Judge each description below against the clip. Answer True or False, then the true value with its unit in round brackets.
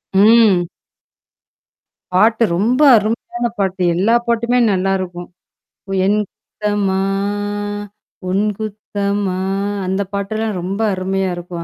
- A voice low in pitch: False (200 Hz)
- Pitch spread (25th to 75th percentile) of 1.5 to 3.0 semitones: True (2.6 semitones)